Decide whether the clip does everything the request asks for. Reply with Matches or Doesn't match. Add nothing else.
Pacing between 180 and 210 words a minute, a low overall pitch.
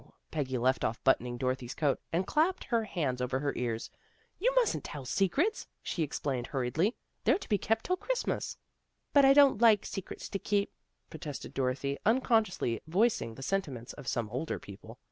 Doesn't match